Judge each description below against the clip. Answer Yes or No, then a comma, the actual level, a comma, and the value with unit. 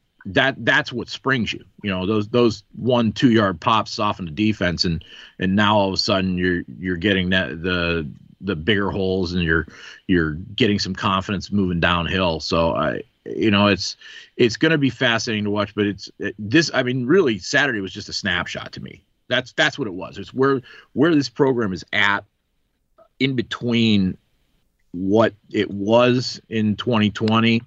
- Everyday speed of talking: Yes, average, 180 wpm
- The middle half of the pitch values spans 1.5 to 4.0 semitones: Yes, average, 3.7 semitones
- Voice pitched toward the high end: No, low, 105 Hz